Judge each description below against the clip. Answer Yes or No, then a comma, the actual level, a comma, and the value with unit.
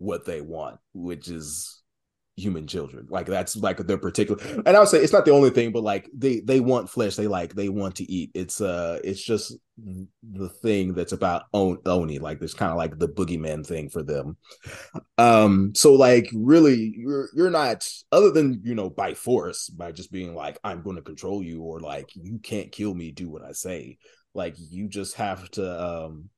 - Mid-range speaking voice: No, low, 100 Hz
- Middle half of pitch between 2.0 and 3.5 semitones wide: No, average, 4.6 semitones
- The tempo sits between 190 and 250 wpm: Yes, average, 200 wpm